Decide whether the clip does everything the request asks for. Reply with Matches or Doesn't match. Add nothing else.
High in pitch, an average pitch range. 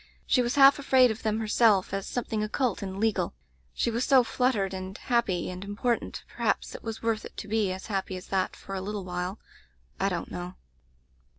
Matches